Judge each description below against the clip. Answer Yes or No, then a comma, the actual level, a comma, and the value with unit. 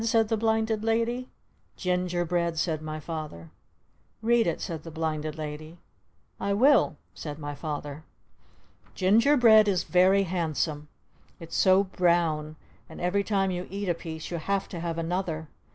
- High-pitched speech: No, medium, 175 Hz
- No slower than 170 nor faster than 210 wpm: No, average, 155 wpm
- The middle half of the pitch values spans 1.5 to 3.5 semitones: No, average, 4.2 semitones